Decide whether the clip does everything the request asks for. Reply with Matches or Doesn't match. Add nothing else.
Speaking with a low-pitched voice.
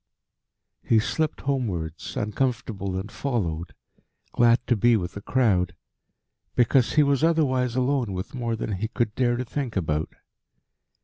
Matches